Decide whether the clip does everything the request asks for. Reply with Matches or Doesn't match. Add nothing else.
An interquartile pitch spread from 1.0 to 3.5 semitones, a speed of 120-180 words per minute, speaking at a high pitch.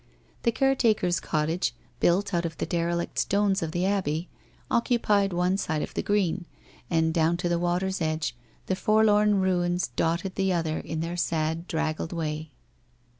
Doesn't match